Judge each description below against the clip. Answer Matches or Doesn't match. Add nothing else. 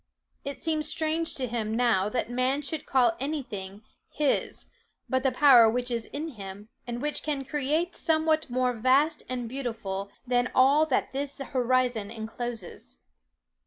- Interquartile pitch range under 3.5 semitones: Doesn't match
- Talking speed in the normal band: Matches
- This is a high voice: Matches